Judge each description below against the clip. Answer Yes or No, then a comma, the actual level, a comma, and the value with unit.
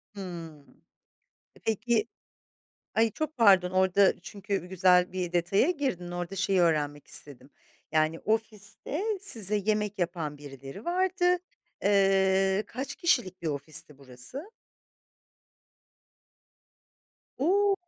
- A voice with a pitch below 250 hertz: Yes, high, 190 Hz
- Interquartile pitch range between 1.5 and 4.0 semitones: No, average, 4.7 semitones